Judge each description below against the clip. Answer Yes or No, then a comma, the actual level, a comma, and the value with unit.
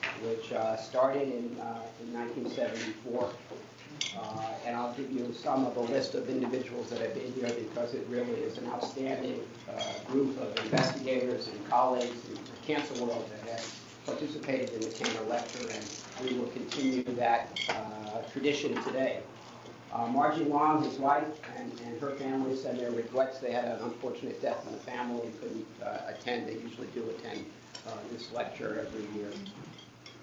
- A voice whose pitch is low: Yes, low, 125 Hz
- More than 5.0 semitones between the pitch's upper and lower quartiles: No, narrow, 2.4 semitones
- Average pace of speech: Yes, average, 170 wpm